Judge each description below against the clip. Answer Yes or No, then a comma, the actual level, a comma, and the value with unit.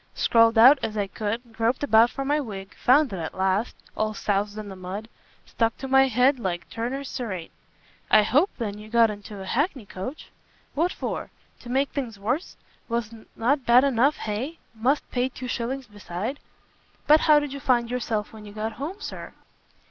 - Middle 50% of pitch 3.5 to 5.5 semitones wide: Yes, average, 4.2 semitones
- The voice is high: Yes, high, 235 Hz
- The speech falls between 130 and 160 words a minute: No, average, 185 wpm